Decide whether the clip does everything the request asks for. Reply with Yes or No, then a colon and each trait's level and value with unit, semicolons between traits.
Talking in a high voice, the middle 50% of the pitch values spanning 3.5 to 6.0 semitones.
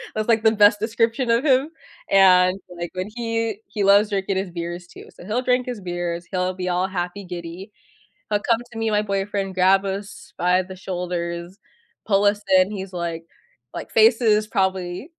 No: high, 195 Hz; average, 3.1 semitones